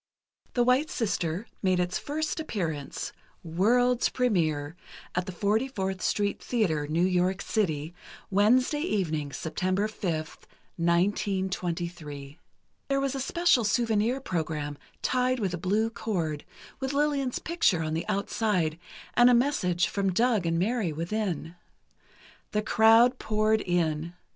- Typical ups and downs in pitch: No, wide, 6.0 semitones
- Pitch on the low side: No, high, 195 Hz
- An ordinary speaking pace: No, slow, 125 wpm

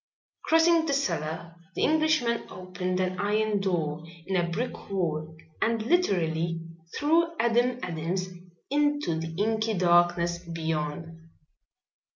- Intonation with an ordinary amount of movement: No, wide, 6.3 semitones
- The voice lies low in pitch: No, medium, 185 Hz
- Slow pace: Yes, slow, 115 wpm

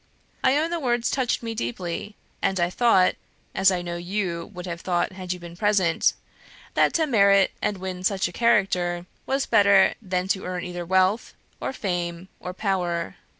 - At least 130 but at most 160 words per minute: No, average, 180 wpm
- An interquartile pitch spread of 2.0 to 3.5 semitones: Yes, average, 2.9 semitones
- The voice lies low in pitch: No, medium, 185 Hz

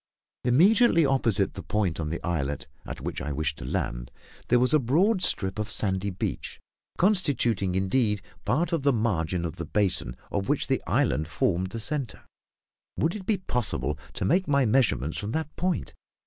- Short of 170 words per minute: No, average, 175 wpm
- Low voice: Yes, low, 105 Hz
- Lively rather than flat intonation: Yes, wide, 9.0 semitones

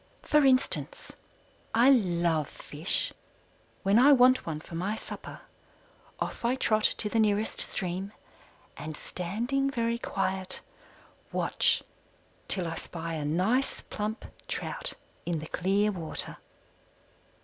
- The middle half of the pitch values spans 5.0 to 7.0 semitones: Yes, wide, 5.6 semitones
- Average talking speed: No, slow, 120 wpm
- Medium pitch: No, high, 200 Hz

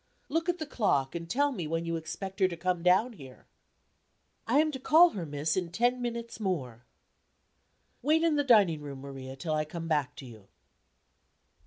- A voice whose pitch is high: No, medium, 180 Hz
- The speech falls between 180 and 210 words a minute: Yes, average, 190 wpm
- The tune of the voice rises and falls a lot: Yes, wide, 8.2 semitones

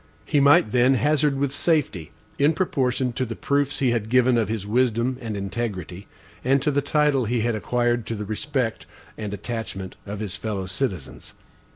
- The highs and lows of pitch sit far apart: No, average, 4.4 semitones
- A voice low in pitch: Yes, low, 120 Hz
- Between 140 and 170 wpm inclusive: No, average, 180 wpm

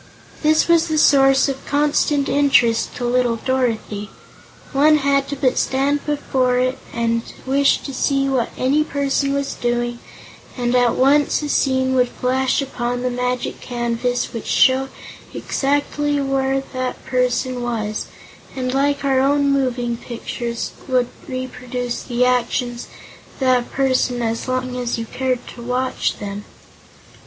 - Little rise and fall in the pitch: Yes, narrow, 2.1 semitones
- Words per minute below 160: Yes, average, 145 wpm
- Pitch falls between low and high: No, very high, 255 Hz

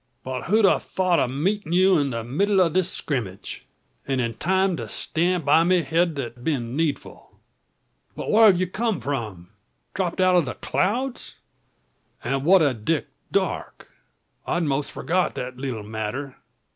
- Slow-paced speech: No, average, 165 wpm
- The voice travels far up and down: Yes, wide, 6.2 semitones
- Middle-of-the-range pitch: Yes, medium, 160 Hz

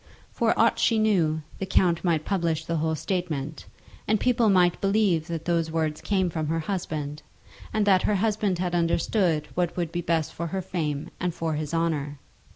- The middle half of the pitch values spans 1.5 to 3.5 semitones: Yes, average, 3.1 semitones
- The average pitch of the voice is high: No, medium, 170 Hz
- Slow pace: No, average, 185 wpm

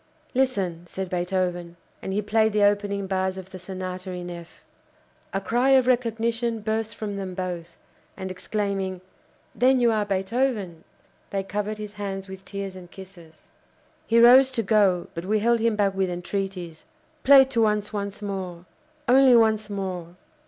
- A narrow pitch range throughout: No, average, 3.0 semitones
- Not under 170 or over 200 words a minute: No, average, 160 wpm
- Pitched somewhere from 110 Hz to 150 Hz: No, high, 200 Hz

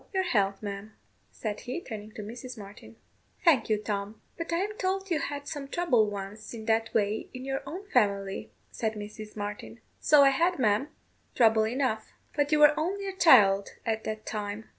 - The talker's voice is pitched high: Yes, high, 225 Hz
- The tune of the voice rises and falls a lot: Yes, wide, 5.8 semitones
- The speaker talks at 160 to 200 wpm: Yes, average, 185 wpm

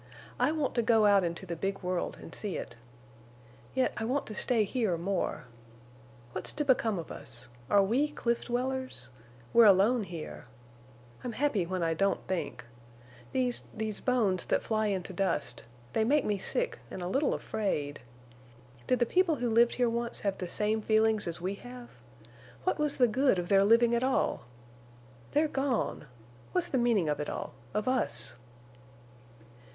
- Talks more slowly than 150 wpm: No, average, 165 wpm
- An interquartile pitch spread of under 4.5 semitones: No, average, 5.2 semitones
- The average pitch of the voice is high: Yes, high, 215 Hz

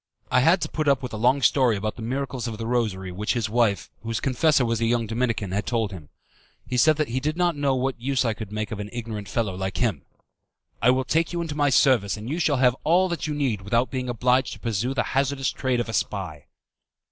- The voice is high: No, low, 120 Hz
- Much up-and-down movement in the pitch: No, average, 3.9 semitones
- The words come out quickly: Yes, fast, 250 wpm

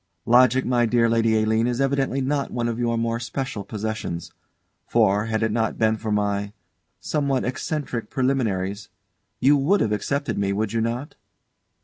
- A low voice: Yes, low, 115 Hz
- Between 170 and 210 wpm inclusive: No, average, 160 wpm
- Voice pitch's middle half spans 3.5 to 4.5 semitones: No, average, 3.1 semitones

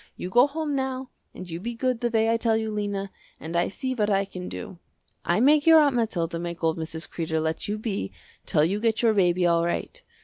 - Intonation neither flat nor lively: No, wide, 5.7 semitones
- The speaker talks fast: Yes, fast, 235 wpm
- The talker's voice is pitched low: No, high, 210 Hz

